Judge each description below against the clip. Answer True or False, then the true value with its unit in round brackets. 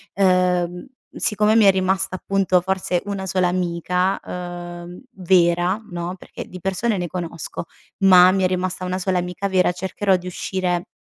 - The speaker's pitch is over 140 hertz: True (185 Hz)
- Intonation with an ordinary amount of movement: False (1.3 semitones)